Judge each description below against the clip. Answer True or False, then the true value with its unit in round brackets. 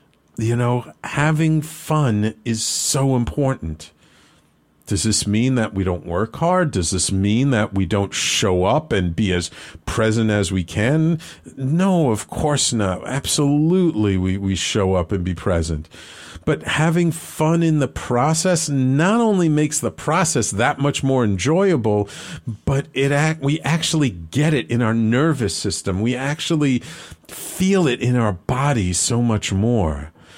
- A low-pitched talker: True (115 Hz)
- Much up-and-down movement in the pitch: True (7.6 semitones)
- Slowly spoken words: False (155 wpm)